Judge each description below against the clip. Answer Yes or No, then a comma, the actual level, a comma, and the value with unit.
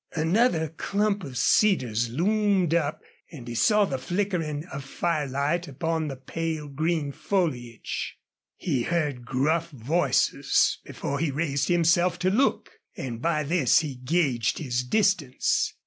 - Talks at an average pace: No, slow, 130 wpm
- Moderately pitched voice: Yes, medium, 155 Hz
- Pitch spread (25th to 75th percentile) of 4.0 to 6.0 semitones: Yes, average, 4.4 semitones